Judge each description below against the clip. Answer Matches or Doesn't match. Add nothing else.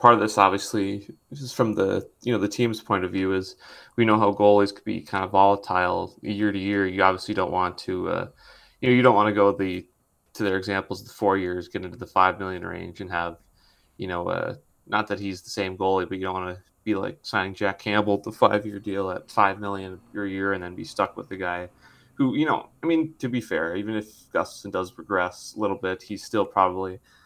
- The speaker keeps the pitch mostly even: Matches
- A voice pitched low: Matches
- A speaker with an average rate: Doesn't match